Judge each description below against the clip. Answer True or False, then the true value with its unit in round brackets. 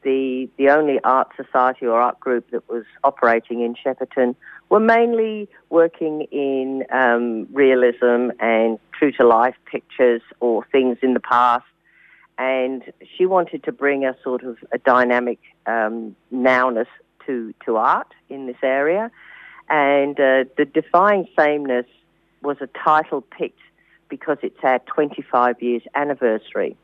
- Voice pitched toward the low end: True (130 Hz)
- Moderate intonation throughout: True (3.0 semitones)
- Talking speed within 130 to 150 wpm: True (140 wpm)